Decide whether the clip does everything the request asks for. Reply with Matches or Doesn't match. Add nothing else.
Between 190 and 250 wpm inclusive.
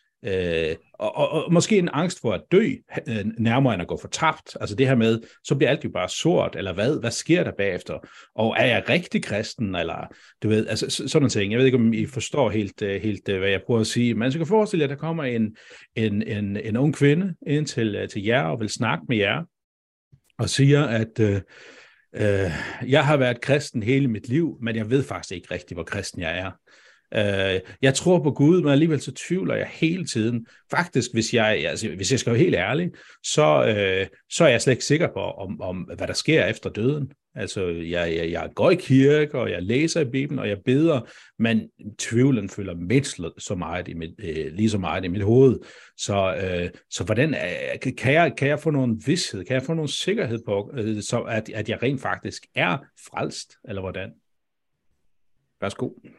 Matches